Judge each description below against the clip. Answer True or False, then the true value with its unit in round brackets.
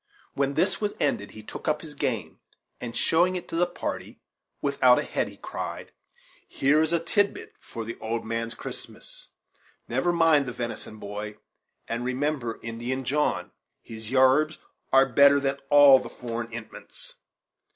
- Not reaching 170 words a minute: True (160 wpm)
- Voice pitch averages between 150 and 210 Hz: False (130 Hz)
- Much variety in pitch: False (4.5 semitones)